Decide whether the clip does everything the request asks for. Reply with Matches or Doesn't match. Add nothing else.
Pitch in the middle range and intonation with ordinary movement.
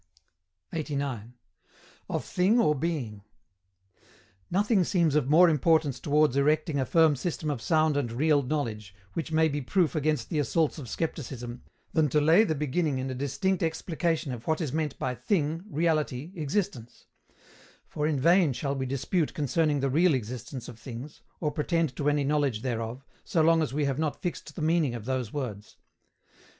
Matches